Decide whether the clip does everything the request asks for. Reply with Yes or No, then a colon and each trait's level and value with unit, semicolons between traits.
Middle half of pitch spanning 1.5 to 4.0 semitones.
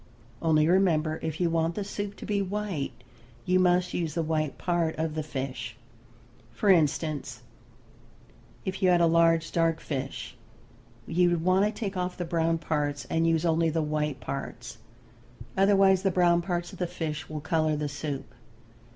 Yes: average, 2.8 semitones